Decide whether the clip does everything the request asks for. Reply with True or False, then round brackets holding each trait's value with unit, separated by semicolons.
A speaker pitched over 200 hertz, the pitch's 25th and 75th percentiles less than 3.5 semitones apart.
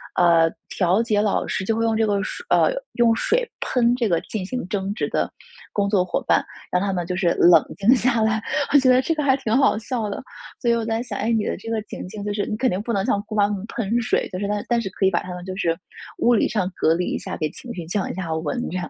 False (210 Hz; 3.8 semitones)